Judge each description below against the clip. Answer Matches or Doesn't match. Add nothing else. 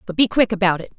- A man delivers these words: Doesn't match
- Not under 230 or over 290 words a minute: Doesn't match